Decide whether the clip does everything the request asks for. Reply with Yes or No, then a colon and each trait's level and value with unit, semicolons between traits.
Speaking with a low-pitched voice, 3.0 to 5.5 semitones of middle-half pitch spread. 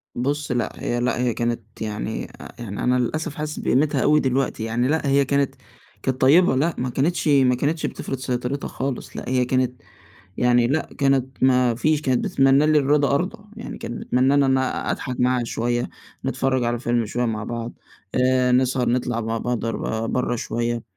No: low, 130 Hz; narrow, 2.6 semitones